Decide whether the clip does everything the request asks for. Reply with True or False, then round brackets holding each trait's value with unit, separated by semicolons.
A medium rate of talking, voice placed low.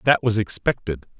True (150 wpm; 105 Hz)